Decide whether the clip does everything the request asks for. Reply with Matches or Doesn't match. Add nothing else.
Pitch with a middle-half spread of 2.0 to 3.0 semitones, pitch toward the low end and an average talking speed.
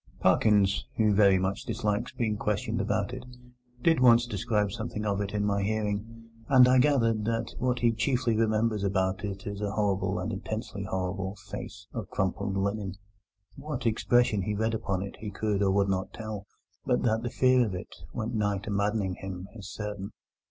Matches